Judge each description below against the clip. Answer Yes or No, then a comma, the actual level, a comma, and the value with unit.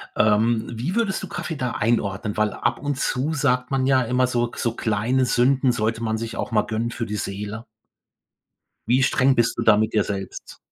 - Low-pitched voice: Yes, low, 120 Hz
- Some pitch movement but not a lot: Yes, average, 3.1 semitones